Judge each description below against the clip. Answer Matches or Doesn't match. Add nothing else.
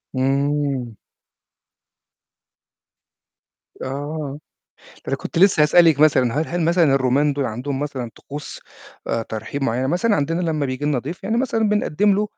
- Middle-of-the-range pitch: Matches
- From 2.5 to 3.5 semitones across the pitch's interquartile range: Doesn't match